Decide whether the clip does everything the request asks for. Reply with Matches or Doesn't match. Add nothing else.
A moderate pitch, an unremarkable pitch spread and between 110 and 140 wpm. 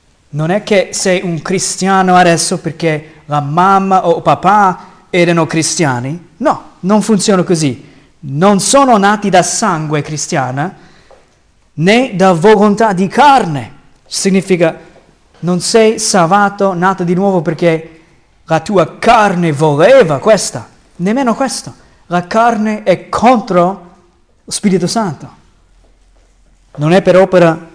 Matches